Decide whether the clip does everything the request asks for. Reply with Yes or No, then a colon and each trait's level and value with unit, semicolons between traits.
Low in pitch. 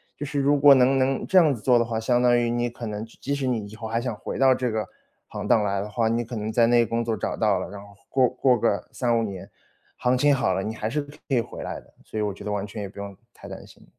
Yes: low, 115 Hz